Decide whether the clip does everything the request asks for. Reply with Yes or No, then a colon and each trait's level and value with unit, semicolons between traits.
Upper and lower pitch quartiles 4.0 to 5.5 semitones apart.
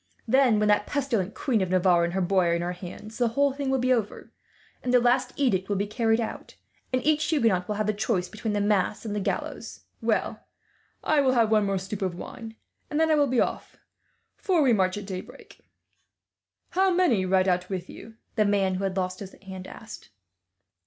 Yes: average, 5.0 semitones